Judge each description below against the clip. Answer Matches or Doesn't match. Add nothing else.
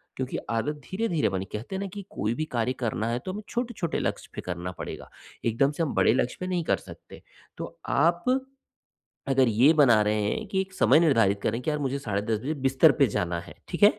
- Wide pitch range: Matches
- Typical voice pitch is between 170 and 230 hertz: Doesn't match